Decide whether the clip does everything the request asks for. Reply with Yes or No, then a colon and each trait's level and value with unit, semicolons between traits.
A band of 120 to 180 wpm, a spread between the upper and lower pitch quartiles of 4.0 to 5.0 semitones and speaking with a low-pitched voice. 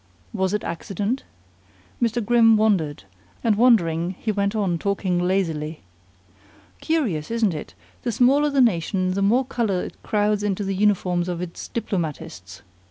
No: average, 145 wpm; average, 4.4 semitones; high, 200 Hz